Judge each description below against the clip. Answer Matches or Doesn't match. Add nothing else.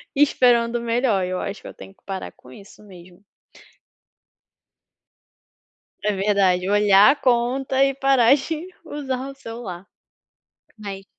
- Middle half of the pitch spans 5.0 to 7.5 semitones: Matches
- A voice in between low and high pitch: Doesn't match